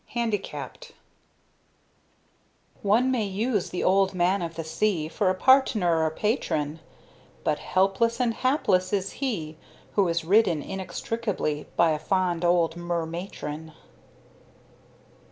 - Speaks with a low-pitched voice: No, medium, 185 Hz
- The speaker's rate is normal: No, slow, 120 wpm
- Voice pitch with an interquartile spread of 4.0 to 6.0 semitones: Yes, average, 4.4 semitones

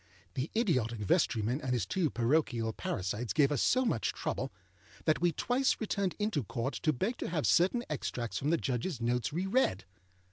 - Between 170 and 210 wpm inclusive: Yes, average, 180 wpm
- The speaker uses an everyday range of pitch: No, wide, 7.7 semitones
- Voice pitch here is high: No, medium, 145 Hz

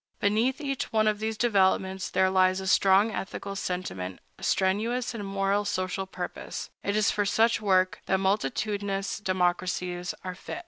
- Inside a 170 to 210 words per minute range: No, average, 155 wpm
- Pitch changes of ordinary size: No, narrow, 2.2 semitones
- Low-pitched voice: No, high, 195 Hz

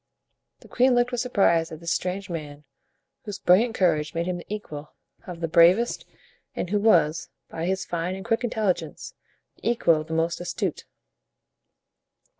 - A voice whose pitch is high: No, medium, 180 Hz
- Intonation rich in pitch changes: No, average, 4.2 semitones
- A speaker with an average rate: Yes, average, 165 wpm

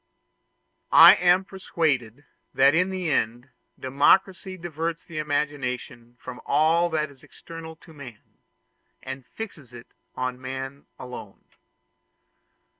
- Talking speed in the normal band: No, slow, 115 wpm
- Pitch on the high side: No, medium, 145 Hz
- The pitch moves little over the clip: No, average, 4.6 semitones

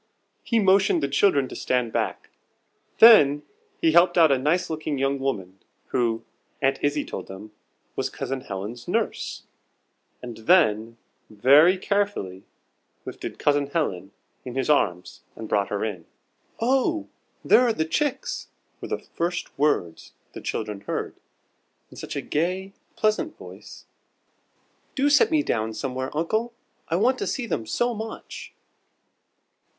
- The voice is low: No, medium, 145 Hz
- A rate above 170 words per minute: No, average, 140 wpm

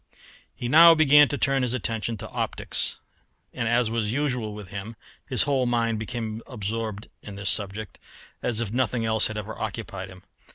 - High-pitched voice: No, low, 115 Hz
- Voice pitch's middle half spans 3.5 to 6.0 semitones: No, average, 2.9 semitones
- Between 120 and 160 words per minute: No, average, 175 wpm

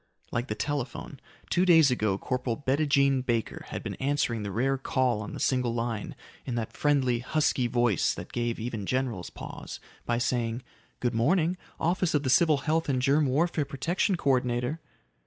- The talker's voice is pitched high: No, low, 130 Hz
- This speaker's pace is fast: No, average, 175 wpm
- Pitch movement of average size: Yes, average, 3.5 semitones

